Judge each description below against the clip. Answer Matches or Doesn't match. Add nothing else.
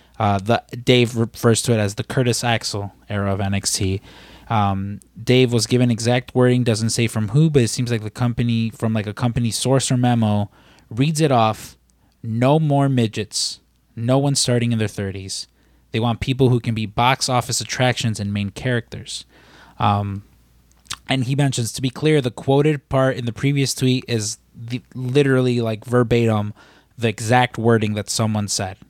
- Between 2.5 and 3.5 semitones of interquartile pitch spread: Matches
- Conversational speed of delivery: Matches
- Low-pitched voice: Matches